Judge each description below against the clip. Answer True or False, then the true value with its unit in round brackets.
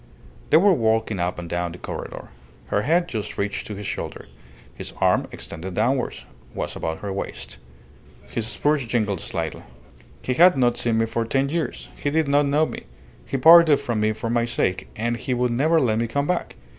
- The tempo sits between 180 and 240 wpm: True (195 wpm)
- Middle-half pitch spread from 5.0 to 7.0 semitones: True (5.3 semitones)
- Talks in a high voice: False (120 Hz)